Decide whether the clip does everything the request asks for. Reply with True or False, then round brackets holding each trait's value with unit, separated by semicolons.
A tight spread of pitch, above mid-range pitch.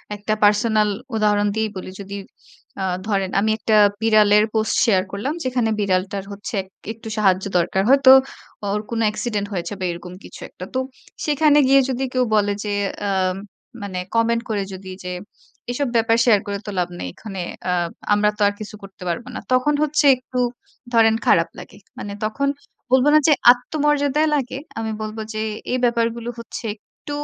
False (3.6 semitones; 215 Hz)